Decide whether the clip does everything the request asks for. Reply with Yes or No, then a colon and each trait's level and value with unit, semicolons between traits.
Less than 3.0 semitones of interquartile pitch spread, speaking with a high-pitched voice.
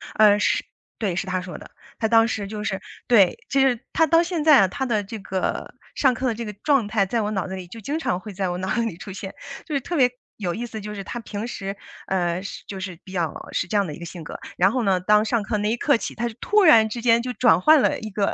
No: average, 3.8 semitones; high, 210 Hz